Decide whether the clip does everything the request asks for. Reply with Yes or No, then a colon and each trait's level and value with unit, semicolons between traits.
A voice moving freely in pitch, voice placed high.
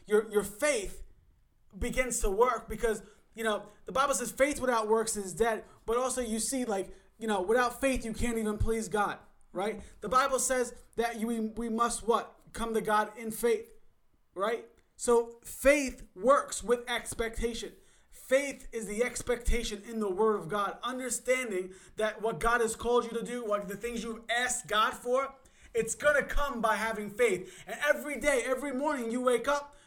No: narrow, 2.6 semitones; high, 230 Hz